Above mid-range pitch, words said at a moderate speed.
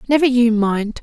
Yes: high, 235 Hz; average, 175 wpm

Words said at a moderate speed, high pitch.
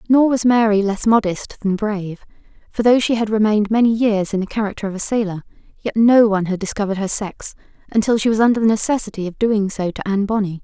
No: fast, 220 wpm; high, 210 Hz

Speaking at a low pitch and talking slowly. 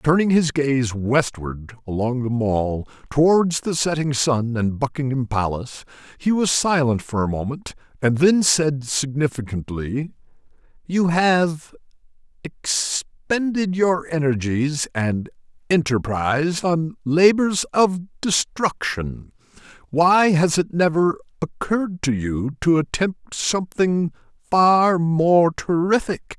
No: medium, 150 Hz; slow, 110 wpm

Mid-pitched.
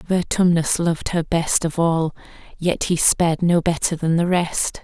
Yes: medium, 165 Hz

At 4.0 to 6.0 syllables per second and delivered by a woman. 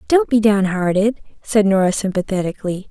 Yes: 5.5 syllables/s; female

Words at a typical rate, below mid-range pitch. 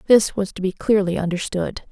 No: average, 190 wpm; high, 195 Hz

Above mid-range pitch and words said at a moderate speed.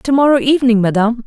Yes: high, 245 Hz; average, 190 wpm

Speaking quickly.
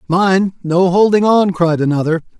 No: average, 150 wpm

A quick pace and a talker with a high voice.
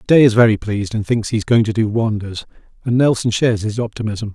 No: fast, 220 wpm; low, 110 Hz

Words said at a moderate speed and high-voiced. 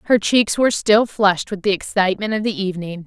No: fast, 215 wpm; high, 200 Hz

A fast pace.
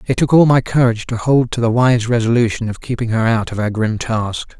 Yes: fast, 250 wpm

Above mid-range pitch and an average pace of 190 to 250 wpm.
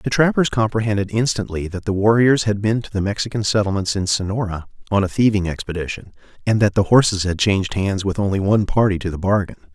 No: low, 100 Hz; fast, 205 wpm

